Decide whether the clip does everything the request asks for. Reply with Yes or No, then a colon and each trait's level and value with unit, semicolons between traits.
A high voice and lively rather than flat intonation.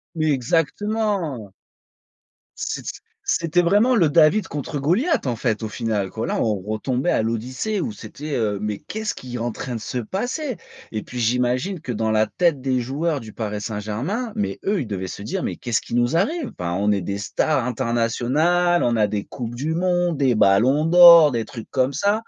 No: low, 130 Hz; wide, 7.6 semitones